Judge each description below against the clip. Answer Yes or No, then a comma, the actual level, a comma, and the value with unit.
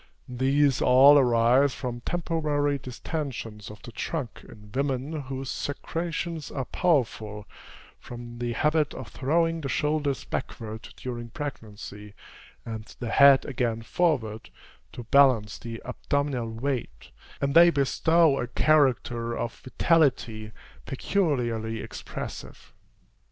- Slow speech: Yes, slow, 115 wpm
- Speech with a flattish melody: No, average, 4.0 semitones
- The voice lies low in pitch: Yes, low, 130 Hz